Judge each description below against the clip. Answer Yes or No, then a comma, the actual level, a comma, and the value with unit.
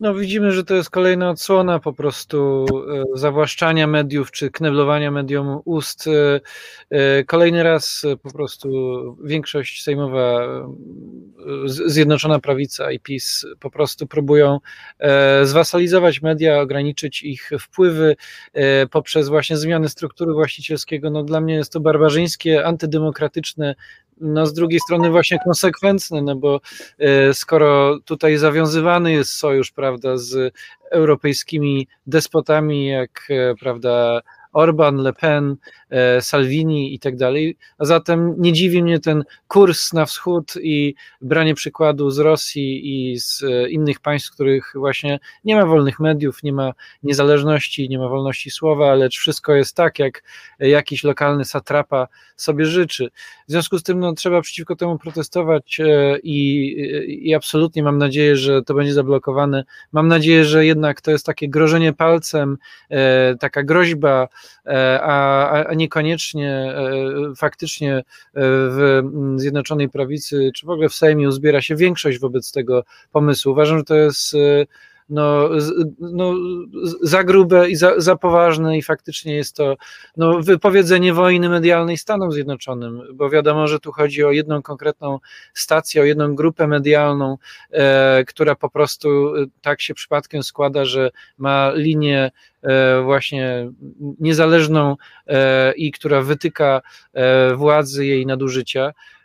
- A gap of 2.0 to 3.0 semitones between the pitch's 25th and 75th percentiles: Yes, narrow, 2.5 semitones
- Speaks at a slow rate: No, average, 135 wpm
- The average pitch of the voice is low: No, medium, 150 Hz